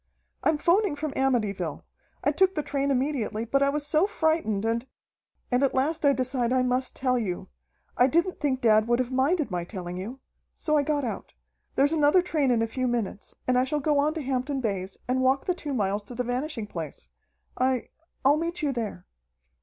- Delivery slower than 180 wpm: No, fast, 205 wpm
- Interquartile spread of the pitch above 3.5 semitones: Yes, average, 4.3 semitones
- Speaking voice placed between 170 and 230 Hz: No, very high, 260 Hz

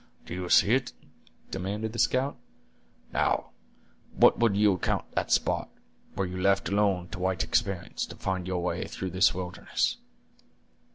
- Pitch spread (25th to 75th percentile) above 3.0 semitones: No, narrow, 2.4 semitones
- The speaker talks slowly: No, average, 155 wpm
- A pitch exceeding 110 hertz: No, very low, 95 Hz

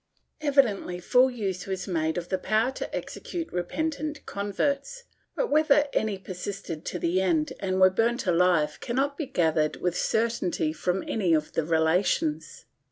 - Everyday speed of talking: Yes, average, 155 wpm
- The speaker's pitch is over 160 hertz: Yes, high, 190 Hz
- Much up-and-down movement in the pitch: Yes, wide, 6.6 semitones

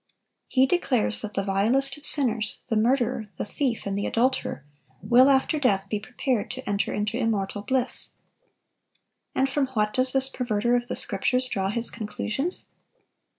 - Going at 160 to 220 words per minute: No, average, 150 wpm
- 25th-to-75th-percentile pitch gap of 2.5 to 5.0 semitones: Yes, average, 4.1 semitones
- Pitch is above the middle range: Yes, high, 235 Hz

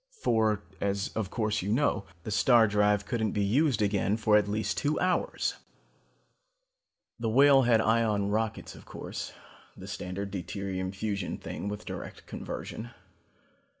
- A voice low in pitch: Yes, low, 105 Hz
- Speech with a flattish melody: Yes, narrow, 2.1 semitones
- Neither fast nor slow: Yes, average, 150 wpm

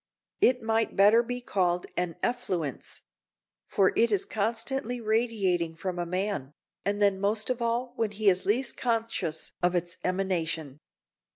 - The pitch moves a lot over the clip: No, average, 4.3 semitones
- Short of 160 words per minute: Yes, average, 150 wpm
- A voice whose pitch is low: No, high, 205 Hz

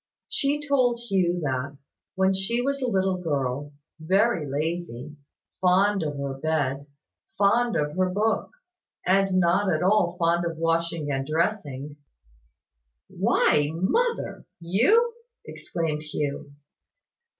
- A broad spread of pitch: No, average, 5.0 semitones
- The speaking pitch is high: No, medium, 175 Hz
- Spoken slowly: Yes, slow, 115 wpm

